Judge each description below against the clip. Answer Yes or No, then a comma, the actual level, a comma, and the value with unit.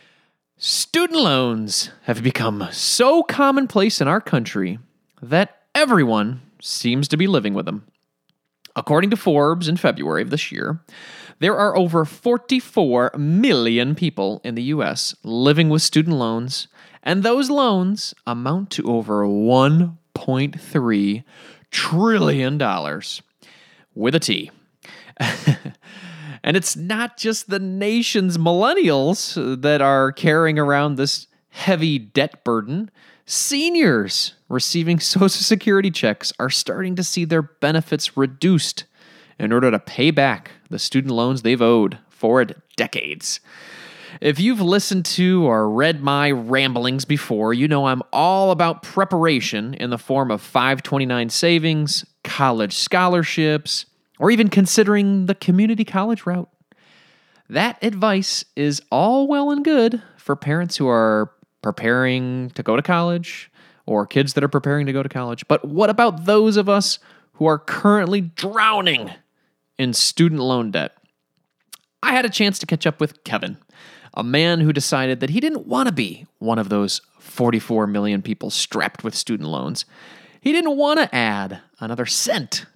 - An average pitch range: No, wide, 7.1 semitones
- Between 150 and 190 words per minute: No, average, 140 wpm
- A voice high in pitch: No, medium, 160 Hz